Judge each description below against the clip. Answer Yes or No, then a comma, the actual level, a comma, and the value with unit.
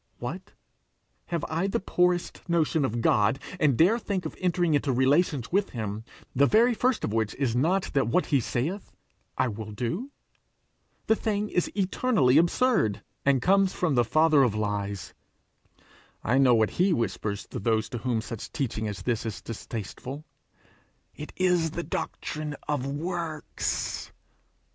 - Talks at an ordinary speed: Yes, average, 160 wpm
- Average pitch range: No, wide, 7.5 semitones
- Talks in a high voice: No, medium, 145 Hz